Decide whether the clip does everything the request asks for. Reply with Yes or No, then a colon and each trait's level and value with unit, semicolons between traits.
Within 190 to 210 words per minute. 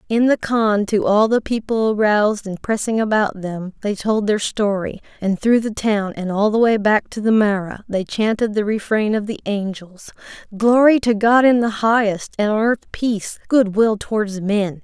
Yes: average, 200 wpm